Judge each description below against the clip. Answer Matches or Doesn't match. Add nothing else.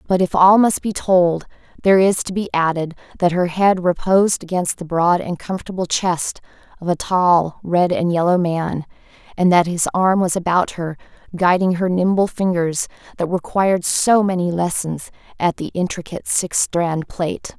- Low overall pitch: Doesn't match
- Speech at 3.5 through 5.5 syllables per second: Matches